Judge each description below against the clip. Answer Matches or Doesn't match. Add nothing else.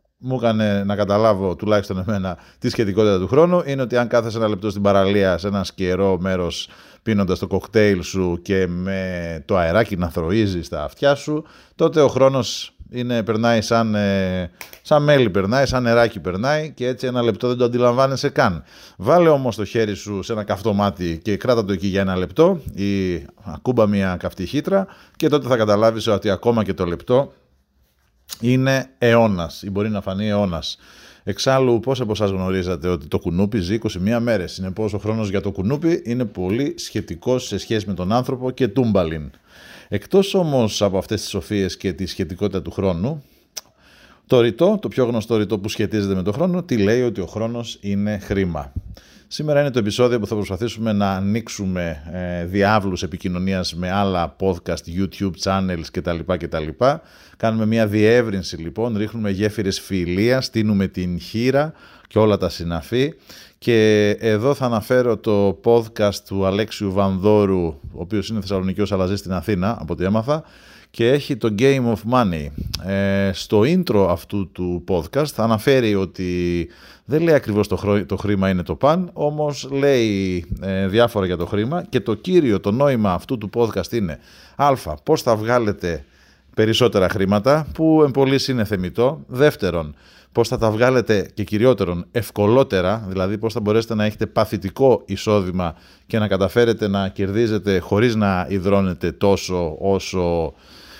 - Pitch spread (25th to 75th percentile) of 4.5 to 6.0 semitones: Doesn't match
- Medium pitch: Doesn't match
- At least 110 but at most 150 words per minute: Doesn't match